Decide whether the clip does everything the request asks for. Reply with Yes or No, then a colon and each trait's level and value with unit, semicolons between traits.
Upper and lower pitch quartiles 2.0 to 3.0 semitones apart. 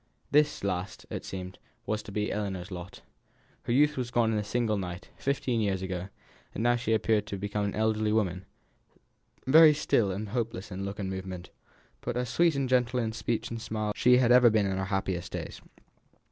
No: average, 4.0 semitones